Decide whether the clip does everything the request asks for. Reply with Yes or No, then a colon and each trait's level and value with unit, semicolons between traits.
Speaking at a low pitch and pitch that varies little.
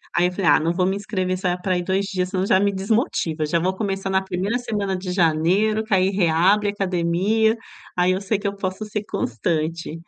No: high, 190 Hz; narrow, 2.2 semitones